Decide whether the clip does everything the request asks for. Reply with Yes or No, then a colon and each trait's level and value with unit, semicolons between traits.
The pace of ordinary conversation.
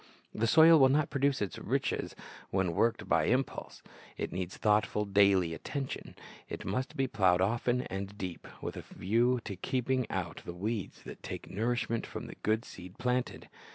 Yes: average, 170 wpm